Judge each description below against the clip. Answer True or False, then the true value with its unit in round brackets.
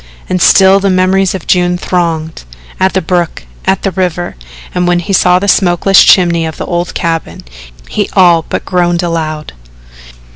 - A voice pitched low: False (175 Hz)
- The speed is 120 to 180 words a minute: True (170 wpm)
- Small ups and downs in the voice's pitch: True (1.8 semitones)